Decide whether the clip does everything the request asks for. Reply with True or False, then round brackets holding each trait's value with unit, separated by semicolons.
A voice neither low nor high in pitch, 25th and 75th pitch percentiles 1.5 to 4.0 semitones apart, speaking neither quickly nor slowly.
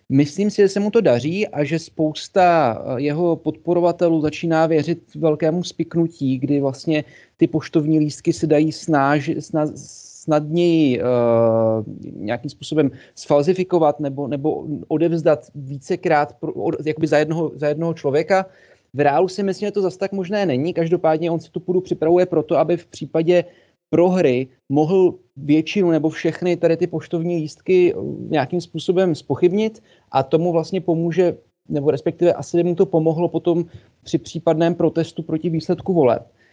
True (165 Hz; 2.7 semitones; 150 wpm)